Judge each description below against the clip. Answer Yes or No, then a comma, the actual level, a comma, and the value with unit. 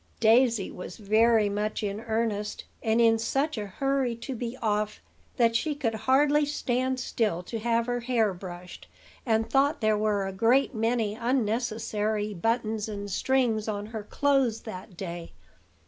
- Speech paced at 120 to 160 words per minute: Yes, average, 155 wpm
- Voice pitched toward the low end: No, high, 225 Hz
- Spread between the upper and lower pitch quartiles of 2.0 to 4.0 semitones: Yes, average, 2.7 semitones